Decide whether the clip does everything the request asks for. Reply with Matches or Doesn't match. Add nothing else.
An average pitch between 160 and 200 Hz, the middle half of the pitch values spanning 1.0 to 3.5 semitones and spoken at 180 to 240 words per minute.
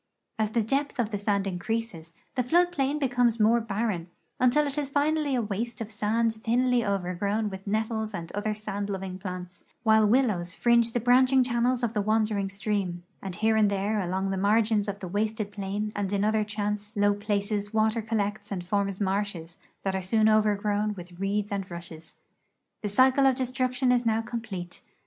Doesn't match